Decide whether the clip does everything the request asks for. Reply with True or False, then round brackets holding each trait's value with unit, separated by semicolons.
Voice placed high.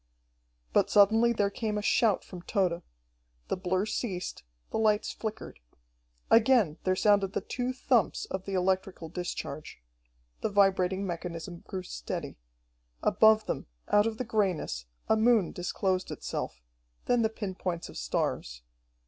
True (195 Hz)